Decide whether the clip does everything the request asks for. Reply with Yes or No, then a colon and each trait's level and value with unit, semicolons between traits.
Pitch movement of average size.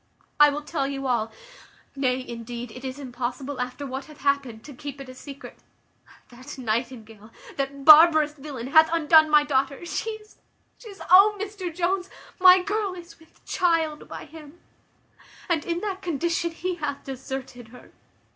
Yes: average, 4.7 semitones